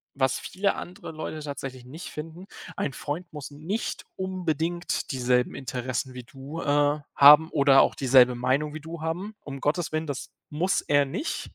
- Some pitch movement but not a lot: Yes, average, 3.4 semitones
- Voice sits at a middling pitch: Yes, medium, 150 Hz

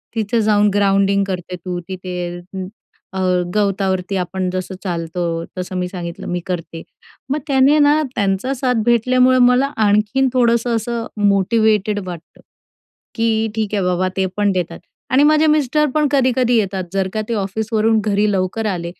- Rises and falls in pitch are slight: No, average, 4.2 semitones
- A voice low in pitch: No, high, 205 Hz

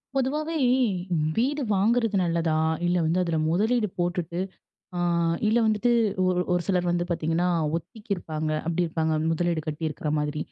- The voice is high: No, medium, 175 Hz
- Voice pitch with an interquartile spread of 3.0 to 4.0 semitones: No, average, 4.7 semitones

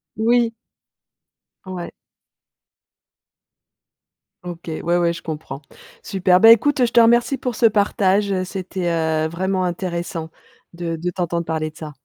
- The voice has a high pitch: No, medium, 180 Hz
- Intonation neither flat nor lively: Yes, average, 3.8 semitones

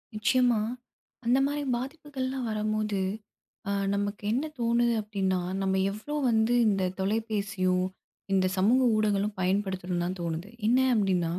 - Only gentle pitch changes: No, average, 3.8 semitones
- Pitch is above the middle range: Yes, high, 210 Hz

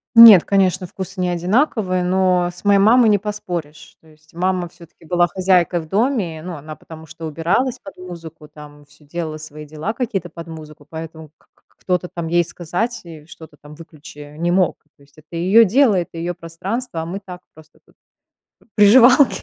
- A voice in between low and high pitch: Yes, medium, 175 Hz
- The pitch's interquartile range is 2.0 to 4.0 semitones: Yes, average, 3.4 semitones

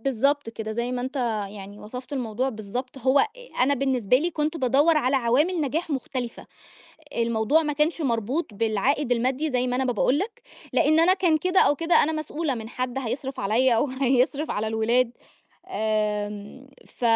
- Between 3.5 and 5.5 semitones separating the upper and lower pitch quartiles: Yes, average, 4.2 semitones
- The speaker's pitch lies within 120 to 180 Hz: No, very high, 255 Hz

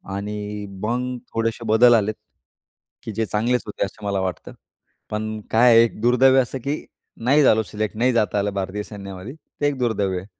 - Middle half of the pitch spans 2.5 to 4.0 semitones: Yes, average, 2.9 semitones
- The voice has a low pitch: Yes, low, 110 Hz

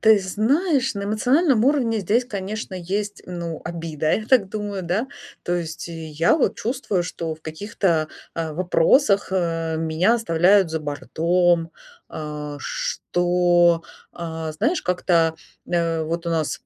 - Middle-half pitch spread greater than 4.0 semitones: Yes, average, 4.5 semitones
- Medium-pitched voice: Yes, medium, 175 Hz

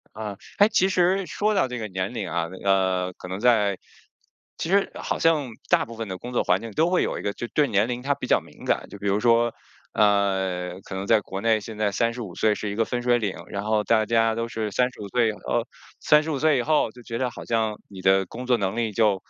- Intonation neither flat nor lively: Yes, average, 3.7 semitones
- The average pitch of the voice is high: No, low, 110 Hz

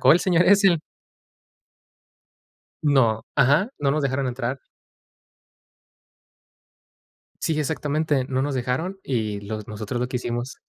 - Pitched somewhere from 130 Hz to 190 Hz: Yes, low, 135 Hz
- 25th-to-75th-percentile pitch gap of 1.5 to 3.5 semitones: No, average, 4.1 semitones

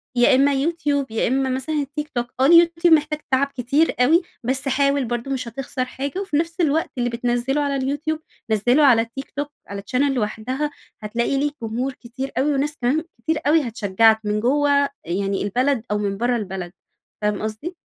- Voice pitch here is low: No, very high, 265 Hz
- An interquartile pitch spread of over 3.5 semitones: Yes, average, 3.9 semitones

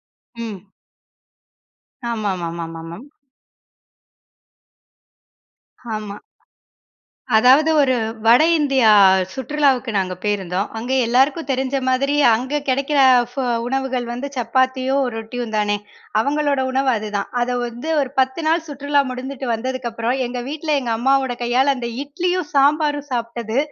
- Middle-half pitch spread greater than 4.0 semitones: No, average, 3.3 semitones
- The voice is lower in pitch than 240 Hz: No, very high, 255 Hz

